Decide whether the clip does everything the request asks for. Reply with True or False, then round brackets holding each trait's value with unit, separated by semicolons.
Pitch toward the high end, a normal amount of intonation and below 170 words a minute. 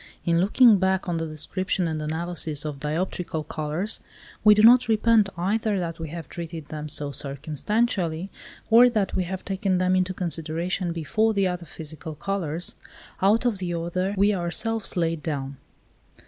False (175 Hz; 3.8 semitones; 160 wpm)